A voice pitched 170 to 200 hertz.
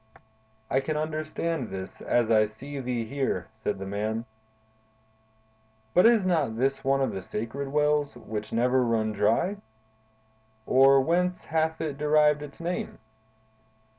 No: low, 135 Hz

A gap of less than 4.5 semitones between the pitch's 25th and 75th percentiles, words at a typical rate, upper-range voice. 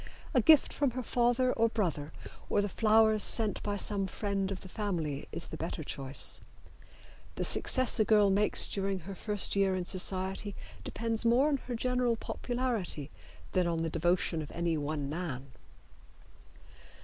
No: average, 4.9 semitones; average, 160 wpm; high, 200 Hz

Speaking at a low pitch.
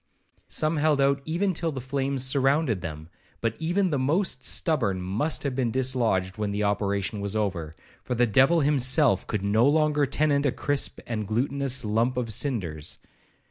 Yes: low, 130 Hz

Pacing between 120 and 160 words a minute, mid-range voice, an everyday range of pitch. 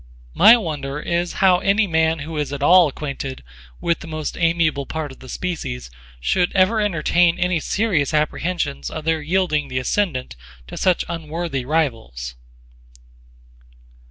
Yes: average, 145 wpm; medium, 160 Hz; average, 4.0 semitones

